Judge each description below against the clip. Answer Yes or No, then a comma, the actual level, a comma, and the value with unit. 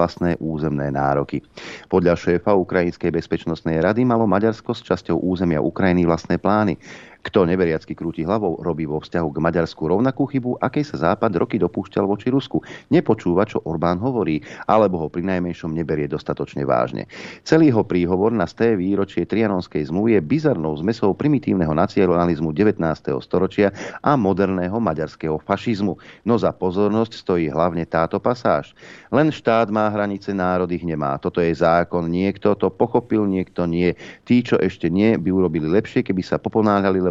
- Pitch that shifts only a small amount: No, average, 4.1 semitones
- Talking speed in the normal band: Yes, average, 155 wpm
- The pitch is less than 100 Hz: Yes, very low, 90 Hz